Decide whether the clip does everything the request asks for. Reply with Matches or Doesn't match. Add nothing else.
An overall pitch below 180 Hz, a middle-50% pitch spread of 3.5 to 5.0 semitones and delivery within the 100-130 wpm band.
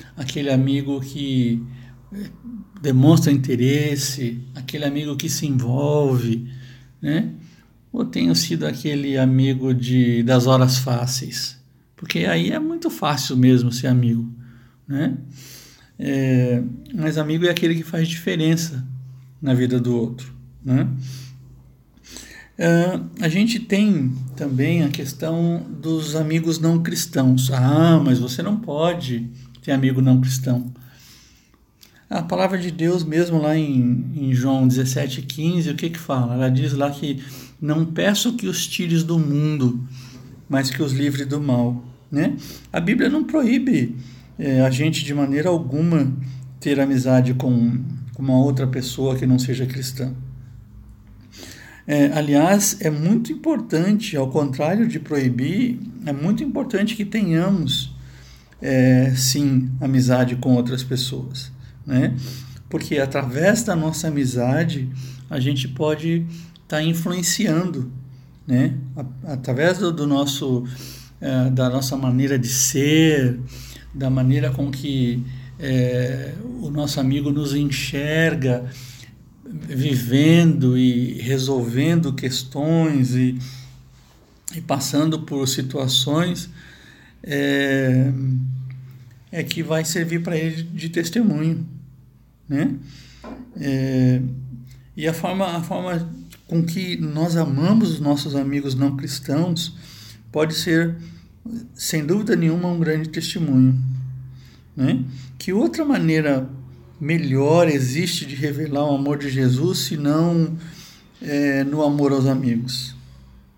Matches